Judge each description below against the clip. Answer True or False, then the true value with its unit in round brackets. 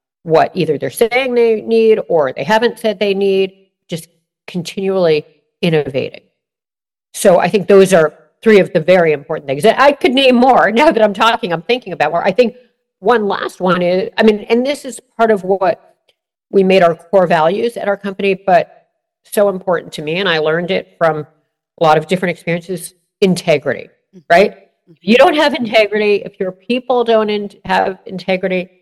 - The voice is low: False (195 Hz)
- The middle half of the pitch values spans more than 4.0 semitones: True (4.4 semitones)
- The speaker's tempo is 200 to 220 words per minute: False (185 wpm)